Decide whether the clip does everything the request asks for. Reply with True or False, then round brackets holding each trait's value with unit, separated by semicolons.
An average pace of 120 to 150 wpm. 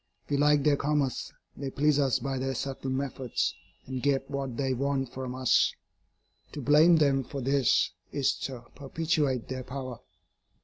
False (160 wpm)